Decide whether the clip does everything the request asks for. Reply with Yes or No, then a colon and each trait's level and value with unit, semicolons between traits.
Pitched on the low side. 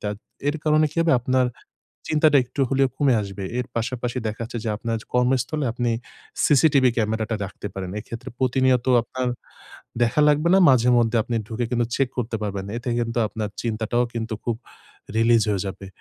Yes: low, 120 Hz